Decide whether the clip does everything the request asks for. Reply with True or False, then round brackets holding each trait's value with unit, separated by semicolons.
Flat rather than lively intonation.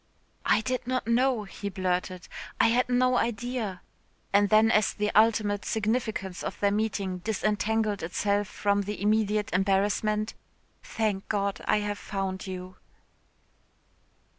True (2.2 semitones)